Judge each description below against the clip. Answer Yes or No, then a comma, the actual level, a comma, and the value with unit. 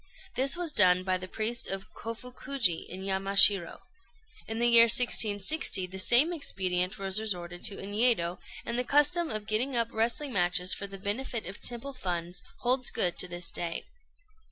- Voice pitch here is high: Yes, high, 210 Hz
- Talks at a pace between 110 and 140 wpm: No, average, 170 wpm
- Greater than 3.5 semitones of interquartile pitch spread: Yes, average, 4.8 semitones